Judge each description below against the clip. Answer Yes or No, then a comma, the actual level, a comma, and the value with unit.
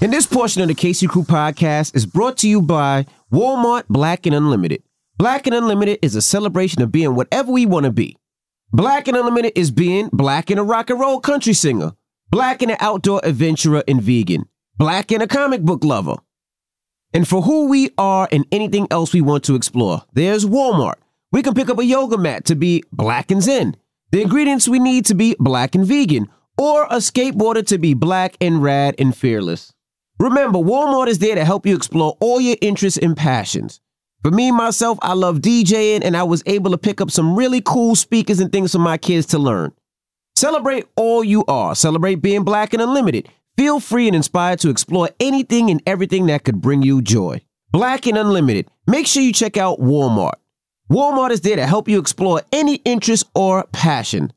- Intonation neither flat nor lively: No, wide, 6.8 semitones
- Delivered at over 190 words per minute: Yes, average, 200 wpm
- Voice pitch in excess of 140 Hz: Yes, high, 190 Hz